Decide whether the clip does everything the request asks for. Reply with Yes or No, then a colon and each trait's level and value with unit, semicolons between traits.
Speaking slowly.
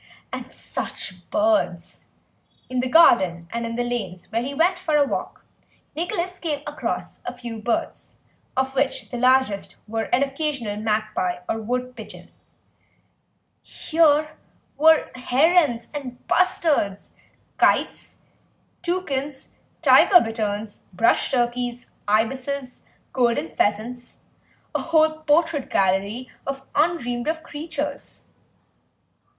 Yes: slow, 110 wpm